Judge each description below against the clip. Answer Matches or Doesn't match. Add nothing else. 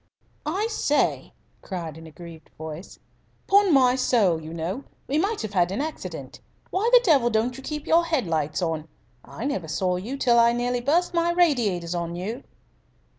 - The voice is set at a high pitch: Matches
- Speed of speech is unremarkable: Matches